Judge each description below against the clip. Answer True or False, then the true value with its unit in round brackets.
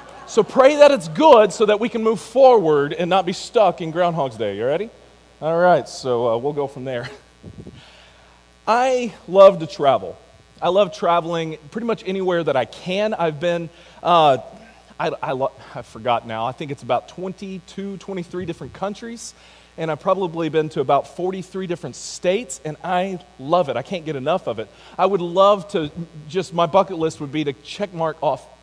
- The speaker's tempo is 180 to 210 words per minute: True (190 wpm)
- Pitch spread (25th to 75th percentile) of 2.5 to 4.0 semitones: False (4.5 semitones)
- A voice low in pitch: False (175 Hz)